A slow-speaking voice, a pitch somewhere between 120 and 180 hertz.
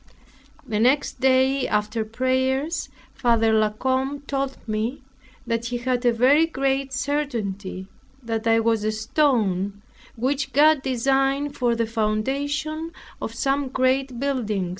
No: slow, 130 wpm; very high, 255 Hz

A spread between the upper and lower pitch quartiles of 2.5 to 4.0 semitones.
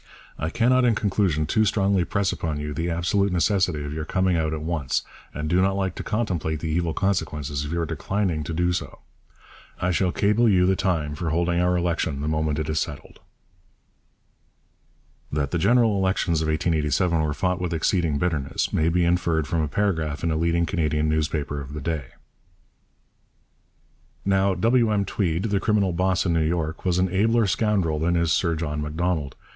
Yes: average, 3.5 semitones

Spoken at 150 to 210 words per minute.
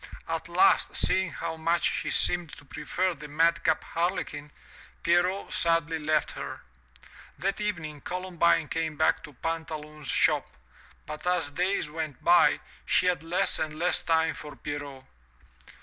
No: average, 140 wpm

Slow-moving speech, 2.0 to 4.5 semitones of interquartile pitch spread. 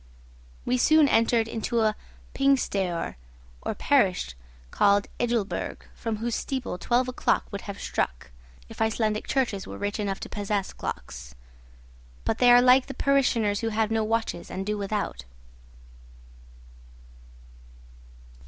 Yes: slow, 130 wpm; average, 3.3 semitones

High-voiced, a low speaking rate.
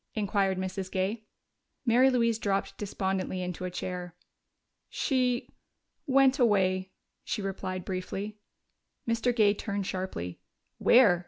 Yes: high, 195 Hz; slow, 110 wpm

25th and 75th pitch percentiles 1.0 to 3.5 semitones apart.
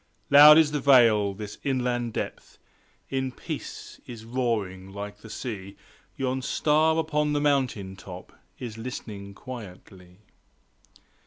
No: average, 5.2 semitones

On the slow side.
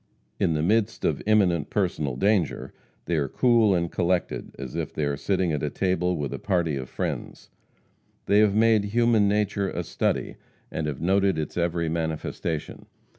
No: average, 175 wpm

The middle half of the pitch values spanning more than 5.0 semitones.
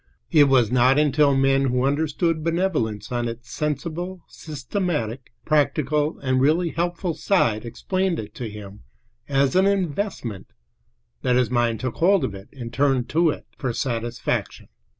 Yes: wide, 5.5 semitones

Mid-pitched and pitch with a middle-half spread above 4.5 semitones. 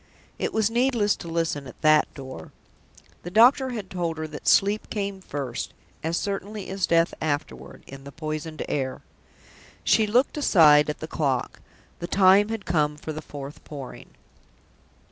Yes: medium, 165 Hz; wide, 5.5 semitones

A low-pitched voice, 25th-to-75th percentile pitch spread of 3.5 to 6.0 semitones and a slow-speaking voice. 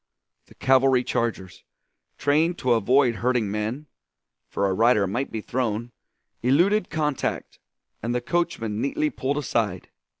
Yes: low, 125 Hz; average, 4.3 semitones; slow, 130 wpm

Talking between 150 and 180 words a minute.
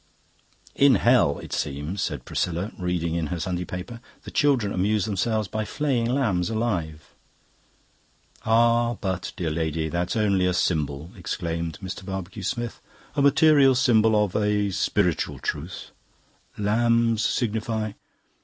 No: slow, 135 wpm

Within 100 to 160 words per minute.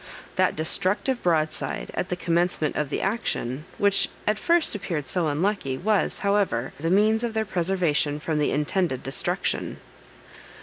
Yes: average, 145 wpm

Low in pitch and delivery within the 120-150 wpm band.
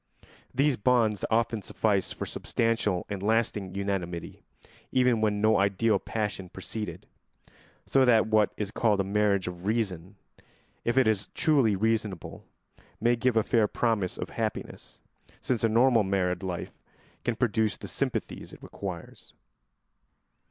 Yes: low, 105 Hz; average, 140 wpm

